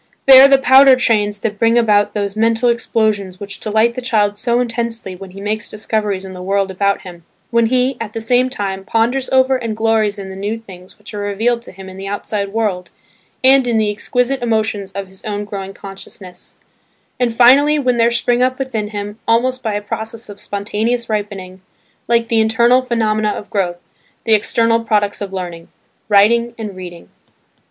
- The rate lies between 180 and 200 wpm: Yes, average, 190 wpm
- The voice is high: Yes, high, 220 Hz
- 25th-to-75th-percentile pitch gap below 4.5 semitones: Yes, average, 2.8 semitones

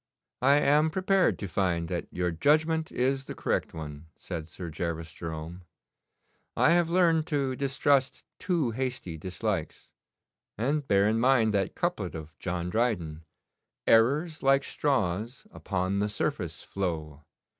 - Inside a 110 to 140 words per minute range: Yes, slow, 135 wpm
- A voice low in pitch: Yes, low, 110 Hz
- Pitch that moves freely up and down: Yes, wide, 8.4 semitones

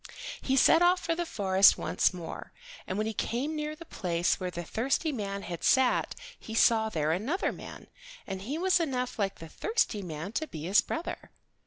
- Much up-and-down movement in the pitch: Yes, wide, 8.6 semitones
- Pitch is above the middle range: Yes, high, 220 Hz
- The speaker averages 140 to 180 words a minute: No, average, 195 wpm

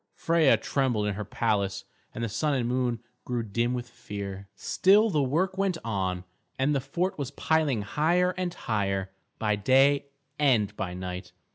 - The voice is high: No, low, 120 Hz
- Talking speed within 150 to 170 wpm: Yes, average, 165 wpm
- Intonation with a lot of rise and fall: Yes, wide, 6.5 semitones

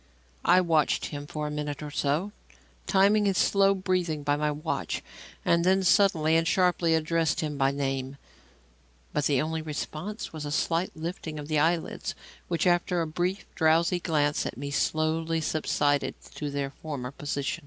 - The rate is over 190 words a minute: No, average, 165 wpm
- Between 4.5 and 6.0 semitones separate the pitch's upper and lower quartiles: No, average, 3.0 semitones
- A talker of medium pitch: Yes, medium, 155 Hz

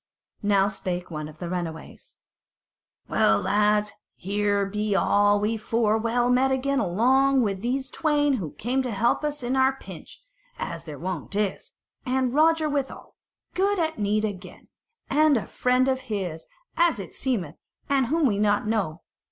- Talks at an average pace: Yes, average, 160 wpm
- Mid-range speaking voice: No, high, 220 Hz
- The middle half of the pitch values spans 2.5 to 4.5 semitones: No, average, 5.1 semitones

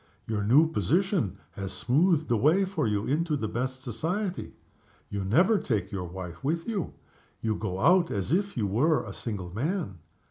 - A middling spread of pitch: No, wide, 8.7 semitones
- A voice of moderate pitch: No, low, 130 Hz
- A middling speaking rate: Yes, average, 175 wpm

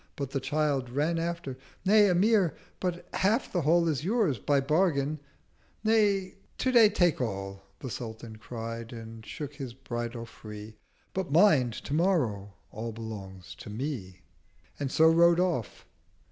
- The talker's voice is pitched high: No, medium, 140 Hz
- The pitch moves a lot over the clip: Yes, wide, 7.2 semitones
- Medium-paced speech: No, slow, 130 wpm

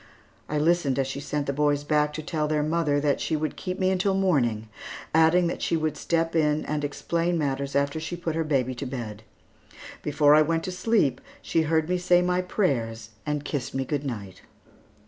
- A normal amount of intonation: Yes, average, 3.2 semitones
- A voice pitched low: No, medium, 150 Hz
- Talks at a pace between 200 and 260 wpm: Yes, fast, 205 wpm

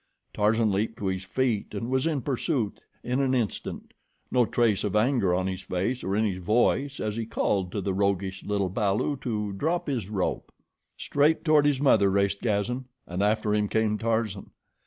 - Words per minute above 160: Yes, average, 185 wpm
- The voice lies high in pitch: No, low, 105 Hz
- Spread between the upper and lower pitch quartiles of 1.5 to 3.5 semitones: No, average, 4.1 semitones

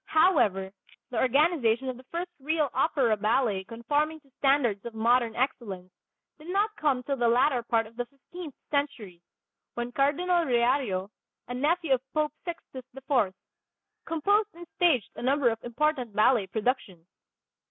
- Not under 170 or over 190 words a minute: No, average, 150 wpm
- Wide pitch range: No, average, 4.8 semitones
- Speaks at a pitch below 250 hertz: No, very high, 260 Hz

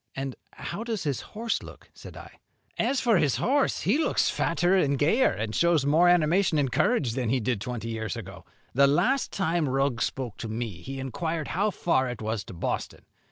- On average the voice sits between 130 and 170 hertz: Yes, medium, 140 Hz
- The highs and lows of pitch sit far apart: Yes, wide, 6.7 semitones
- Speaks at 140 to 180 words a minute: No, average, 200 wpm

